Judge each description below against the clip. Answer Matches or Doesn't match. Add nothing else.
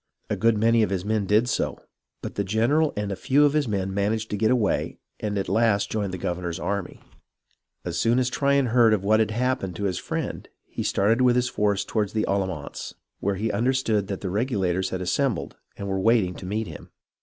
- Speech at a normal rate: Doesn't match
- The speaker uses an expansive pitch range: Doesn't match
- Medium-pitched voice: Doesn't match